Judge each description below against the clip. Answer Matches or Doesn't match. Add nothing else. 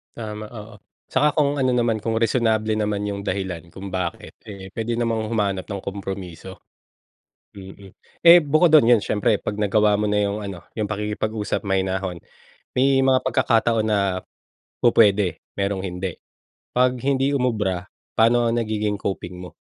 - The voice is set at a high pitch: Doesn't match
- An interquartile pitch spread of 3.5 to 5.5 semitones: Doesn't match